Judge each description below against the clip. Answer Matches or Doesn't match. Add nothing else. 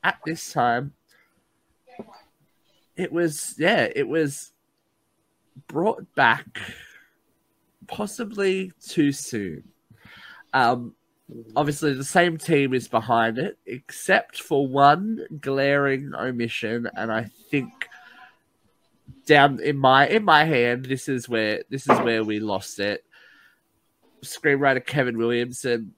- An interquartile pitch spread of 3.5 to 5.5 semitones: Matches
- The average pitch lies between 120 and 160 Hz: Matches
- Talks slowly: Matches